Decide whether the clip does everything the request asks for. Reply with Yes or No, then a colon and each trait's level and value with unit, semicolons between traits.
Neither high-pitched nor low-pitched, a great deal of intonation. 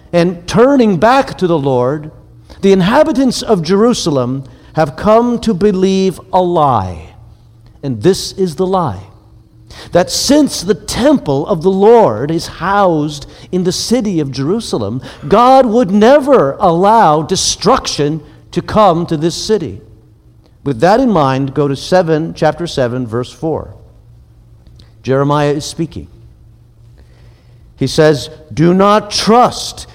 Yes: medium, 160 Hz; wide, 7.7 semitones